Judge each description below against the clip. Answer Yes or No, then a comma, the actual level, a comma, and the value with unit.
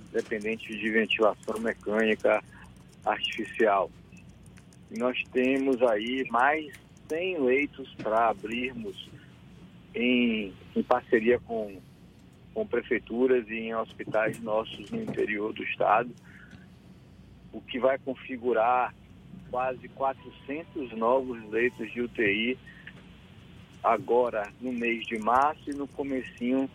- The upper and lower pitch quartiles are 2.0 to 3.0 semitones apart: Yes, average, 2.7 semitones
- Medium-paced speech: No, slow, 105 wpm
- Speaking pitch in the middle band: No, low, 120 Hz